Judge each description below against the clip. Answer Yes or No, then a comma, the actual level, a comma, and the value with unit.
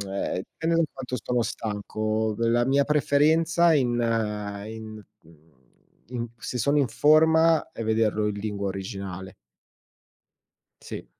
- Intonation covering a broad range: Yes, wide, 6.1 semitones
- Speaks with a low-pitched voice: Yes, low, 115 Hz